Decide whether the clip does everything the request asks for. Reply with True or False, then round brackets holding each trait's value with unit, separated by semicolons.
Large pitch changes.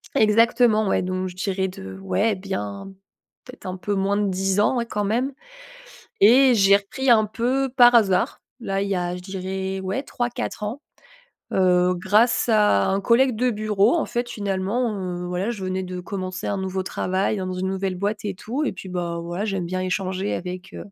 False (2.9 semitones)